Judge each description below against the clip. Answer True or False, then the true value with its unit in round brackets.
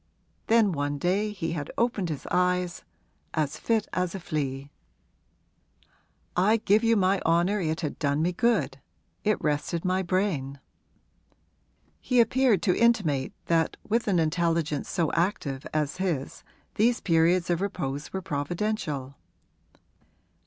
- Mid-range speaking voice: True (175 Hz)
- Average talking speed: False (130 wpm)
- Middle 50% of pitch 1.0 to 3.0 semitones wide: False (5.0 semitones)